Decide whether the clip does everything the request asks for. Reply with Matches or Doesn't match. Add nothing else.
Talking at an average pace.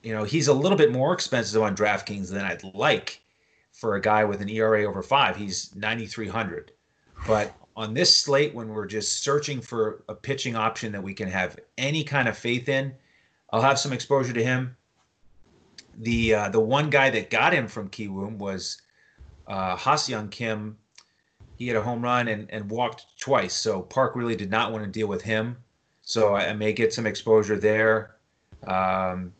Matches